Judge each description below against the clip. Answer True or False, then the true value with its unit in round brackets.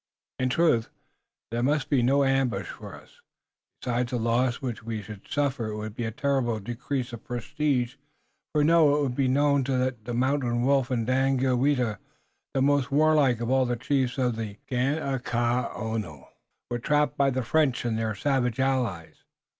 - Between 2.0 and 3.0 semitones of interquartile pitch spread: True (2.7 semitones)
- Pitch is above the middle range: False (125 Hz)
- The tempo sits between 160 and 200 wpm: True (165 wpm)